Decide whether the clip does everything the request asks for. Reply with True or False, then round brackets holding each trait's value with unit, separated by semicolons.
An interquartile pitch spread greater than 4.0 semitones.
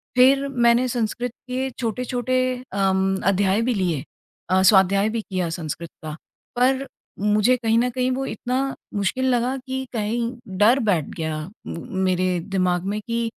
True (4.8 semitones)